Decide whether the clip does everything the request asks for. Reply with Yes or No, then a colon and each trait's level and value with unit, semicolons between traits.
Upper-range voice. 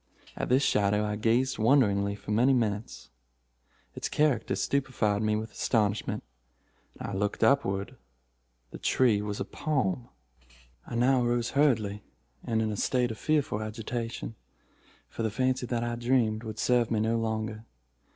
No: low, 115 Hz